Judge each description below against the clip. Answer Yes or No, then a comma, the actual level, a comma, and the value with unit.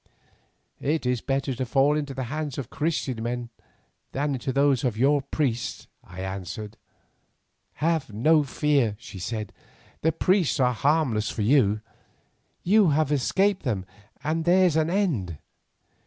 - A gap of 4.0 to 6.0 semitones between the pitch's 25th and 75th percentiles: Yes, average, 5.0 semitones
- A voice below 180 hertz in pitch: Yes, low, 135 Hz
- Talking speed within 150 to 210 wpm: No, average, 140 wpm